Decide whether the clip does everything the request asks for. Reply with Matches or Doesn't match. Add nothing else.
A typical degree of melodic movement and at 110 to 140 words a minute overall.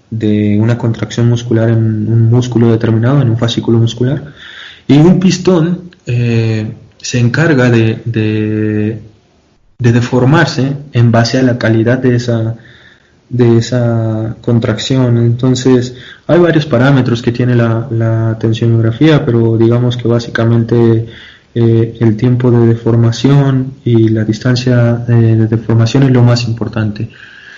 Doesn't match